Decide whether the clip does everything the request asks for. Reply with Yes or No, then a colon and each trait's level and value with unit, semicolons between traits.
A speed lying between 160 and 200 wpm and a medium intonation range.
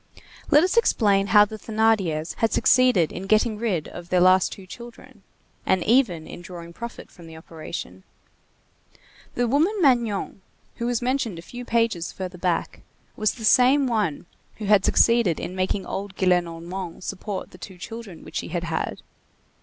Yes: average, 165 wpm; average, 4.9 semitones